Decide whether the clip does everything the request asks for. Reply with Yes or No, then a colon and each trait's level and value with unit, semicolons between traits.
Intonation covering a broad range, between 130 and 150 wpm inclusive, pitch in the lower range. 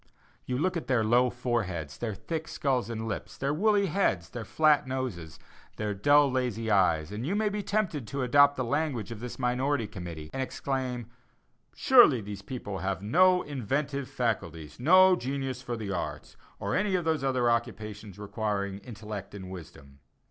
No: wide, 5.8 semitones; average, 170 wpm; low, 120 Hz